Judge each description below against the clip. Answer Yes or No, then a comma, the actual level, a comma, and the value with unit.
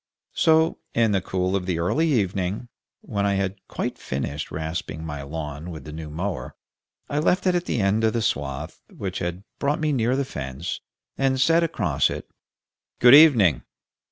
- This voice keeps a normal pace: Yes, average, 180 wpm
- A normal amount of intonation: No, wide, 8.5 semitones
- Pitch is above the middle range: No, very low, 95 Hz